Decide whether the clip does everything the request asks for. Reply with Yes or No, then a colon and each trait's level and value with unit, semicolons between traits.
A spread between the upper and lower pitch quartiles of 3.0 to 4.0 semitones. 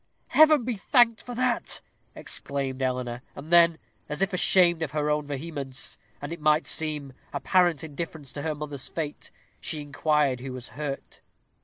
Yes: average, 3.5 semitones